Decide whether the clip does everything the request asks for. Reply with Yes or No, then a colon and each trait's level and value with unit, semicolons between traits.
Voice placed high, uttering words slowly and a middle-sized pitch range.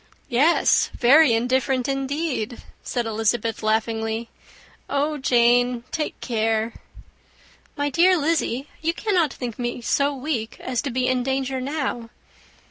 Yes: very high, 255 Hz; slow, 125 wpm; average, 3.6 semitones